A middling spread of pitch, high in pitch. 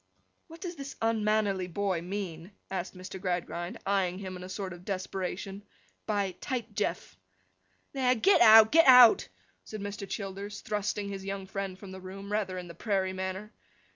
No: narrow, 2.2 semitones; high, 195 Hz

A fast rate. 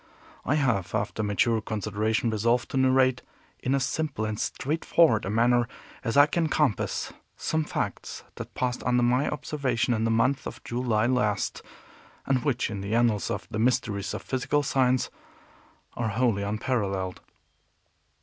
No: average, 150 wpm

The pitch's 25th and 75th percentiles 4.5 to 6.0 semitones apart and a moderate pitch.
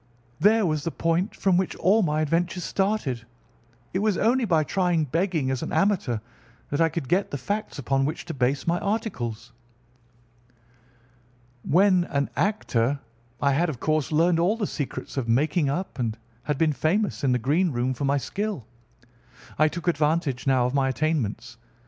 Yes: average, 5.3 semitones; medium, 155 Hz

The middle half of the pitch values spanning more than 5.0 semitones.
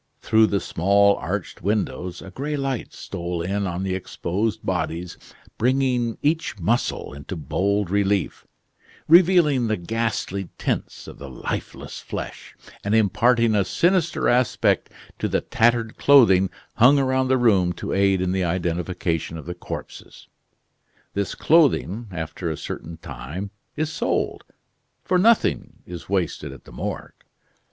Yes: wide, 5.6 semitones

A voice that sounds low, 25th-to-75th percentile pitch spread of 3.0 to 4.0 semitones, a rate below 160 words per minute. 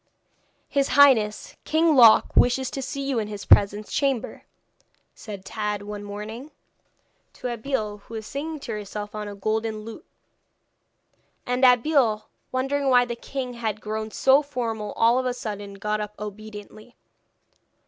No: high, 220 Hz; average, 3.6 semitones; average, 150 wpm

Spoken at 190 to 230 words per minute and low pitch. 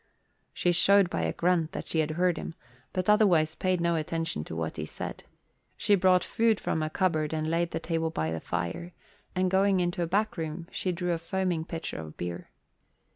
No: fast, 205 wpm; medium, 170 Hz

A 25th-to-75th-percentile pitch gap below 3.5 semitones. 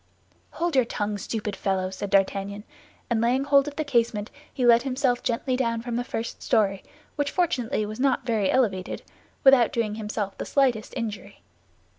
No: average, 3.8 semitones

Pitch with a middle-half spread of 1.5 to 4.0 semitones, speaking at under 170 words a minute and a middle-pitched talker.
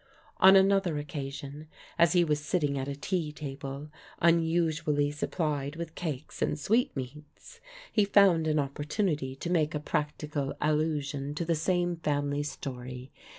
Yes: average, 2.9 semitones; average, 140 wpm; medium, 150 Hz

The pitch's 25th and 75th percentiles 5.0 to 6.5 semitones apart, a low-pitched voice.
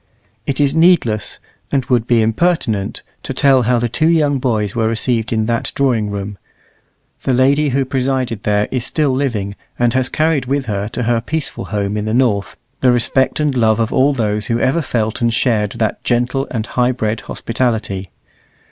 No: average, 3.5 semitones; low, 120 Hz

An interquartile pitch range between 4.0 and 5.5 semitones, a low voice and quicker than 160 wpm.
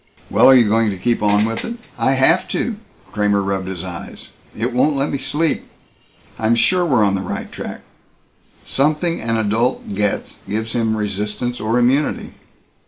Yes: average, 4.3 semitones; low, 115 Hz; average, 170 wpm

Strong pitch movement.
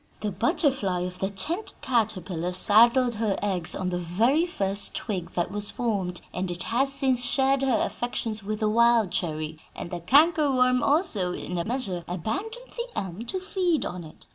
Yes: wide, 6.4 semitones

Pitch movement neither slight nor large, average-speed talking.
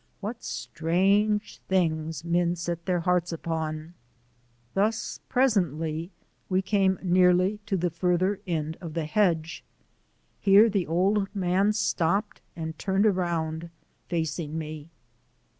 No: average, 3.2 semitones; slow, 115 wpm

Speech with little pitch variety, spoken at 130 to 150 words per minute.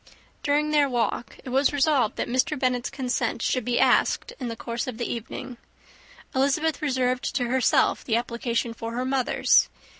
No: narrow, 2.3 semitones; average, 170 wpm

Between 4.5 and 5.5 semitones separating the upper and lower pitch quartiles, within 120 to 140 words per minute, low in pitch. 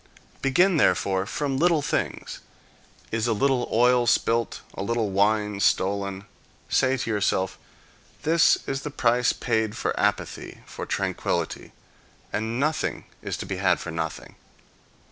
Yes: average, 5.2 semitones; slow, 135 wpm; low, 115 Hz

